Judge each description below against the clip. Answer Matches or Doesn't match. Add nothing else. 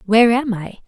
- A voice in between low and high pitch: Doesn't match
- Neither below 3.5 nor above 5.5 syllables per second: Doesn't match